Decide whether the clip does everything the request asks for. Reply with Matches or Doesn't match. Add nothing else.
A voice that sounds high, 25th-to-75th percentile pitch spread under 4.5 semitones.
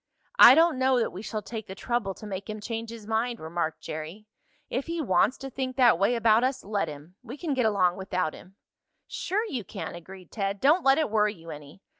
Doesn't match